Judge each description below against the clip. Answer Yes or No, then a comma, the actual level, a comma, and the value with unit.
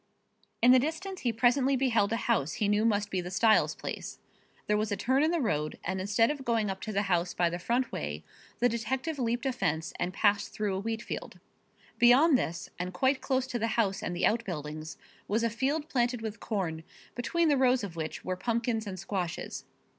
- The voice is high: Yes, high, 225 Hz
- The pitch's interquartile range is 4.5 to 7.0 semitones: Yes, average, 5.0 semitones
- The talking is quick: Yes, fast, 215 wpm